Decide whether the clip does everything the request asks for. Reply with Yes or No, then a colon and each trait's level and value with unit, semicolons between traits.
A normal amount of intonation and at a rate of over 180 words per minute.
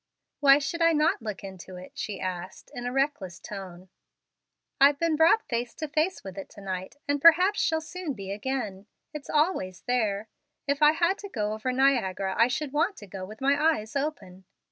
No: wide, 7.6 semitones; average, 195 wpm